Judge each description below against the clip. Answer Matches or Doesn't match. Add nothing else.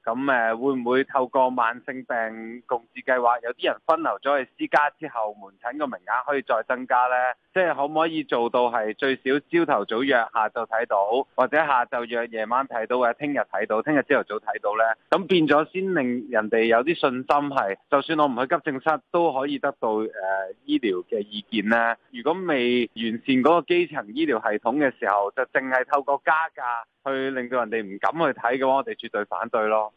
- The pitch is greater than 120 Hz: Matches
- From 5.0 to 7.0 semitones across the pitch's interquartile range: Doesn't match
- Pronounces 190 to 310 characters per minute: Matches